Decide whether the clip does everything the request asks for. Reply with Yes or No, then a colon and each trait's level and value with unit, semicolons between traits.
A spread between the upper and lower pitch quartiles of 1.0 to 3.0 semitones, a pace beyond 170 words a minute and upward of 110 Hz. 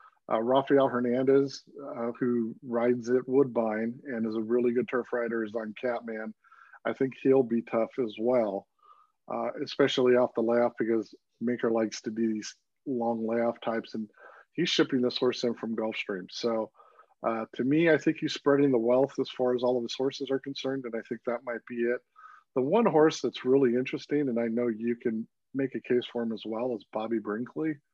Yes: average, 2.7 semitones; average, 200 wpm; low, 120 Hz